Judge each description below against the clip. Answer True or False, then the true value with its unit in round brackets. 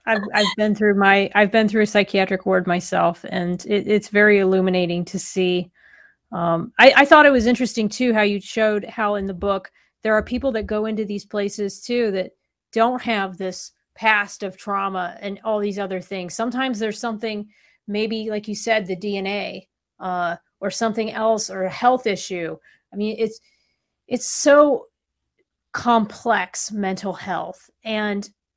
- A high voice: True (210 Hz)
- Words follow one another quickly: False (170 wpm)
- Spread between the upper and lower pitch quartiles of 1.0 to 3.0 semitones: True (2.7 semitones)